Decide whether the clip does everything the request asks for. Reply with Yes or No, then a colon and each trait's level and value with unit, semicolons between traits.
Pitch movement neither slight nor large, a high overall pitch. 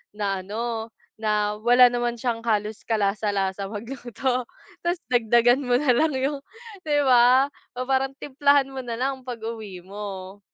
Yes: average, 3.7 semitones; high, 235 Hz